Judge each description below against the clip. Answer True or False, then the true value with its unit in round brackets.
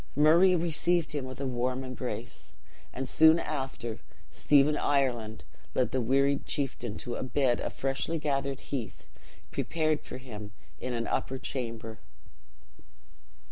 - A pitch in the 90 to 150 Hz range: True (135 Hz)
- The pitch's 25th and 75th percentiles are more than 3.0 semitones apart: True (3.4 semitones)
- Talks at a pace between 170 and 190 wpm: False (135 wpm)